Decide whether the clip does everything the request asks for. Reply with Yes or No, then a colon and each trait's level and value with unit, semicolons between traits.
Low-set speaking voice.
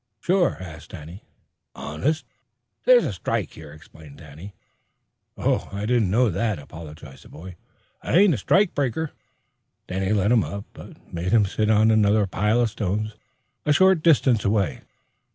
Yes: low, 105 Hz